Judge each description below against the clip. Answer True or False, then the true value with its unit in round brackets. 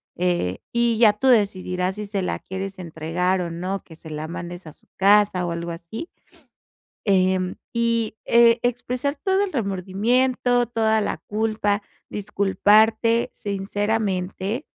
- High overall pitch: True (205 Hz)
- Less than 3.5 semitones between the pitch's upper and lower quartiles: False (4.0 semitones)